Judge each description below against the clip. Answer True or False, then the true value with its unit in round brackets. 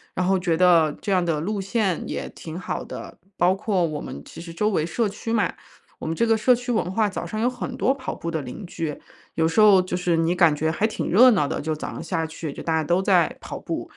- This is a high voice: False (180 Hz)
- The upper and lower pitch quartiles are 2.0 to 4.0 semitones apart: False (4.6 semitones)